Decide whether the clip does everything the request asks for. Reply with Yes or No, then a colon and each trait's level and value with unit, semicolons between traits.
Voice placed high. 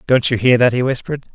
No: low, 125 Hz